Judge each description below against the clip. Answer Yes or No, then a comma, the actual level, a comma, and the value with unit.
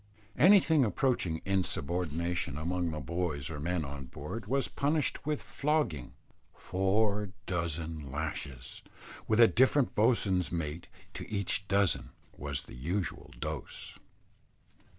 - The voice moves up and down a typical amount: No, wide, 6.0 semitones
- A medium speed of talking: No, slow, 115 wpm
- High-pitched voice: No, very low, 90 Hz